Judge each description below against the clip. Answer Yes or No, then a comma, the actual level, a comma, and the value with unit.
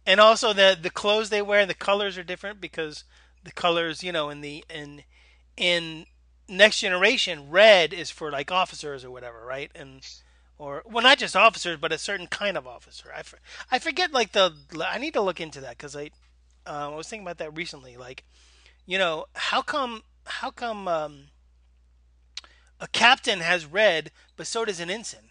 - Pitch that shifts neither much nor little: No, wide, 6.7 semitones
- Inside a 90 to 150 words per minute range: No, average, 190 wpm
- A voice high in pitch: No, medium, 165 Hz